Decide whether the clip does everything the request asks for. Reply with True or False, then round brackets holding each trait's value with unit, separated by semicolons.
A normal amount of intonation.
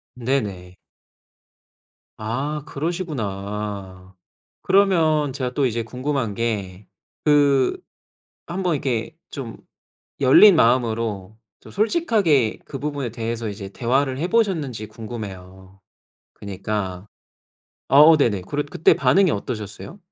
False (6.1 semitones)